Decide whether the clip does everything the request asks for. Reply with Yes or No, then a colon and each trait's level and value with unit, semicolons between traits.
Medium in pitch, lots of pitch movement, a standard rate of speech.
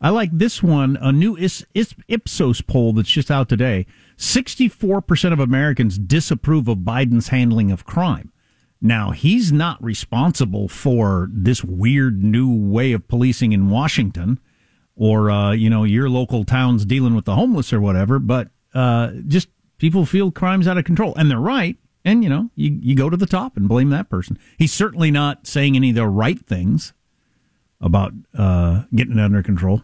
No: low, 125 Hz; wide, 6.3 semitones; average, 175 wpm